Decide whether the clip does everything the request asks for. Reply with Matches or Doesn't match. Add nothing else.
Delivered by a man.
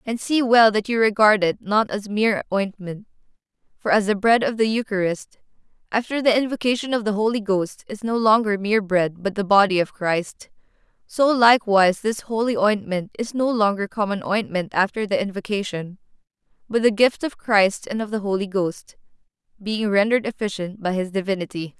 Doesn't match